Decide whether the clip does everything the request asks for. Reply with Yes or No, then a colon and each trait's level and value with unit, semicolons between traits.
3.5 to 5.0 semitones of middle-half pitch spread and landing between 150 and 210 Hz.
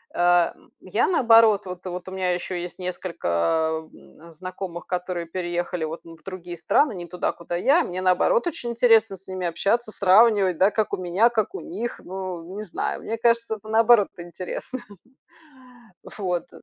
Yes: average, 4.0 semitones; medium, 185 Hz